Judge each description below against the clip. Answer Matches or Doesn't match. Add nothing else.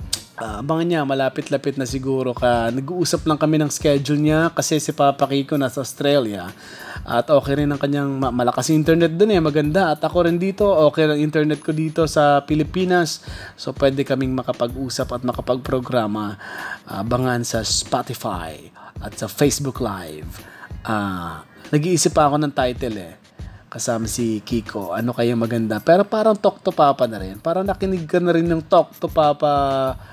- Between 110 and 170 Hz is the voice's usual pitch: Matches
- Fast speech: Matches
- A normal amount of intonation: Matches